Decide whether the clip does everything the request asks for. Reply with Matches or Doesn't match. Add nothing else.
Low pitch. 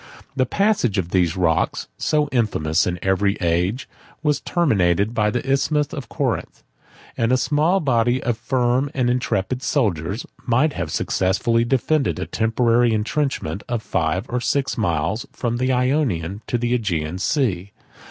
Matches